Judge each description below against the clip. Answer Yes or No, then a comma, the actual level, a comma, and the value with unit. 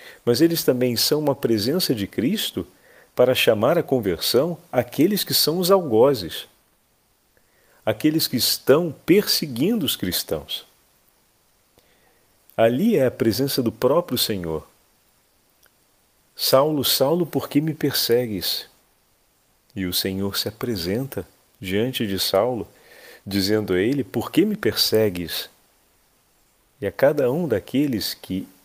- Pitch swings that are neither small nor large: No, wide, 6.7 semitones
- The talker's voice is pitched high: No, low, 125 Hz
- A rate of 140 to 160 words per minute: No, slow, 120 wpm